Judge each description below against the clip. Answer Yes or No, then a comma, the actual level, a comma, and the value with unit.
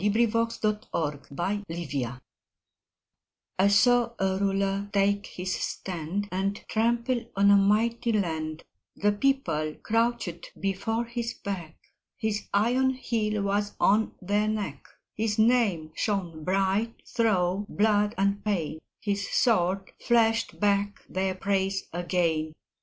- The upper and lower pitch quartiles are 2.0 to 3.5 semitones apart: Yes, average, 3.1 semitones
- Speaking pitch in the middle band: No, high, 200 Hz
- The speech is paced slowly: Yes, slow, 120 wpm